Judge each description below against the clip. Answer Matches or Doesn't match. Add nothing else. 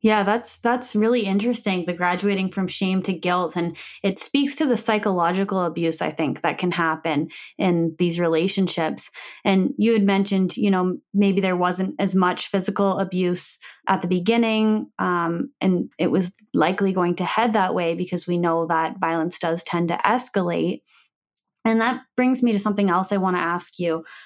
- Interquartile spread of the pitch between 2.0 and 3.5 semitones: Matches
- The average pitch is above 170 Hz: Matches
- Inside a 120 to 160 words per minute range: Doesn't match